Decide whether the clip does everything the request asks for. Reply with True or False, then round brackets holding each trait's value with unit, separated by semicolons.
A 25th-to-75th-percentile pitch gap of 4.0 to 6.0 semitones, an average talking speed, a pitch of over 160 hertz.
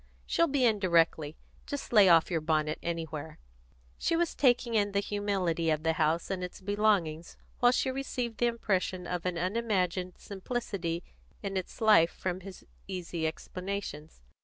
True (4.4 semitones; 160 wpm; 185 Hz)